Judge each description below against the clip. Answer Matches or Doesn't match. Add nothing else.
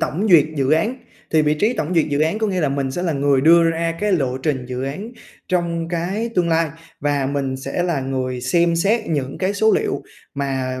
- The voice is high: Doesn't match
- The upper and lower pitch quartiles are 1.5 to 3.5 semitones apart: Doesn't match